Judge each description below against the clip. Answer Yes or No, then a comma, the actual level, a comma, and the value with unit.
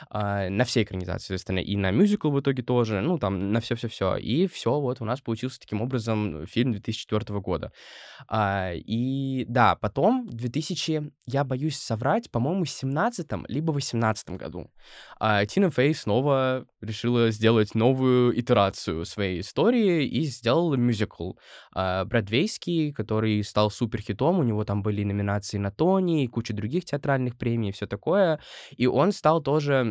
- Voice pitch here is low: Yes, low, 120 Hz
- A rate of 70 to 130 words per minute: No, average, 155 wpm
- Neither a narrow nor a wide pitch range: Yes, average, 5.0 semitones